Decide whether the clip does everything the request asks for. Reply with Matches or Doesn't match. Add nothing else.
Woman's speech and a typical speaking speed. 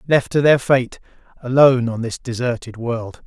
Doesn't match